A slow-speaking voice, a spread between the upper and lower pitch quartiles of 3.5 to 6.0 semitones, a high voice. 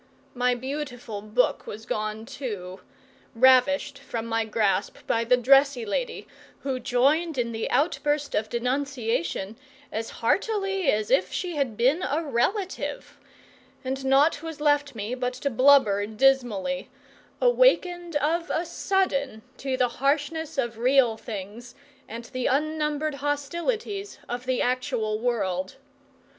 Yes: slow, 130 wpm; average, 4.3 semitones; very high, 260 Hz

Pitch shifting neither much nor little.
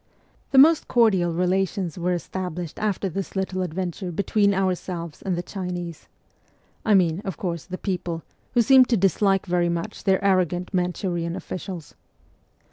No: narrow, 2.1 semitones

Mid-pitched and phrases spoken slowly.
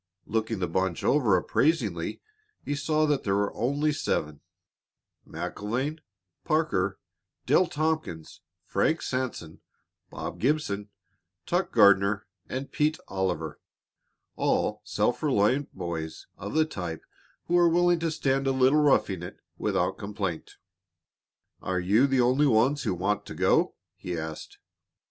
No: low, 120 Hz; slow, 130 wpm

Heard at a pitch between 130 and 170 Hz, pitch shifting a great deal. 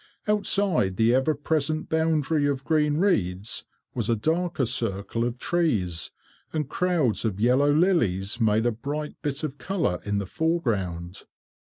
Yes: medium, 140 Hz; wide, 7.1 semitones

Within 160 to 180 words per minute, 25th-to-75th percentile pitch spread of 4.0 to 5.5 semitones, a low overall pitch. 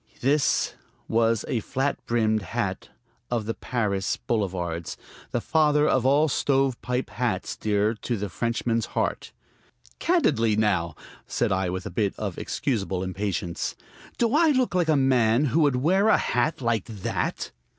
No: average, 150 wpm; average, 5.2 semitones; low, 115 Hz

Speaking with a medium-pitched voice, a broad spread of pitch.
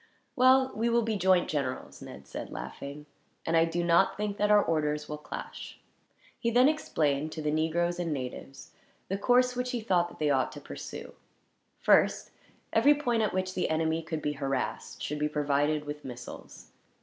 Yes: medium, 165 Hz; wide, 6.0 semitones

